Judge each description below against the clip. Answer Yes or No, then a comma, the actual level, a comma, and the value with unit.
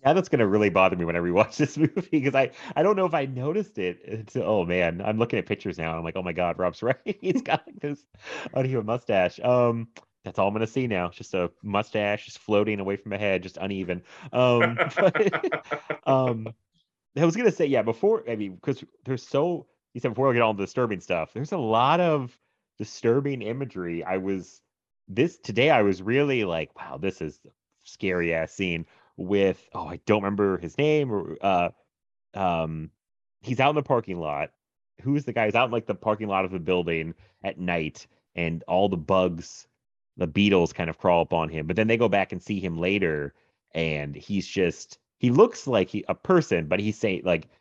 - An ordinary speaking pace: No, fast, 215 wpm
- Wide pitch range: Yes, wide, 6.0 semitones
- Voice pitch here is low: Yes, low, 100 Hz